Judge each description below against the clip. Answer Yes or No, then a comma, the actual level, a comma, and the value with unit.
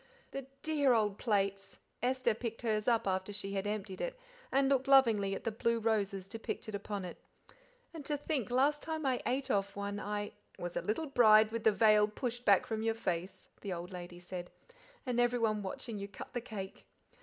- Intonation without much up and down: No, average, 3.8 semitones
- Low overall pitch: No, high, 215 Hz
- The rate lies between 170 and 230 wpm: Yes, average, 200 wpm